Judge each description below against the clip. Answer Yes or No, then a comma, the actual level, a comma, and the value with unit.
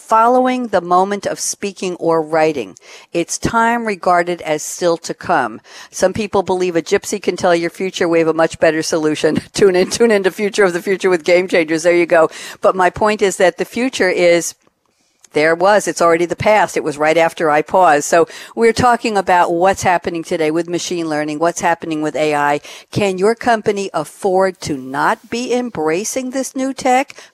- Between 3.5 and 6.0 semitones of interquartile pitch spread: Yes, average, 3.9 semitones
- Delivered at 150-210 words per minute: Yes, average, 195 wpm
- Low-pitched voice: No, medium, 180 Hz